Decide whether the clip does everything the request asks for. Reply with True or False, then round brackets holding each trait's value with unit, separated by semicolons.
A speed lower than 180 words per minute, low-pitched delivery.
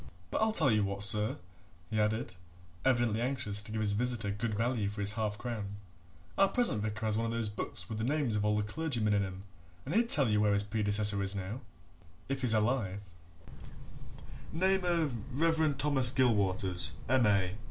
False (185 wpm; 110 Hz)